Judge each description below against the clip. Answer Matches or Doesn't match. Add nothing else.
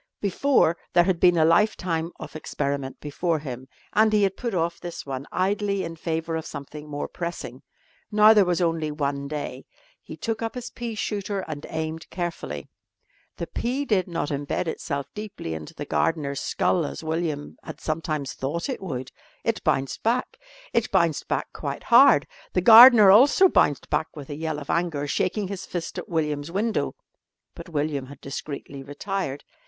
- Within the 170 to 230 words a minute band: Matches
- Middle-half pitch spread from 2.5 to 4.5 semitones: Doesn't match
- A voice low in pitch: Doesn't match